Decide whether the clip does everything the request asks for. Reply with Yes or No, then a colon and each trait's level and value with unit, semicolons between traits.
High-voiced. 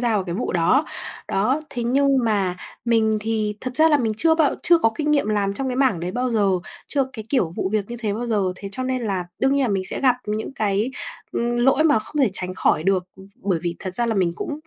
Yes: high, 225 Hz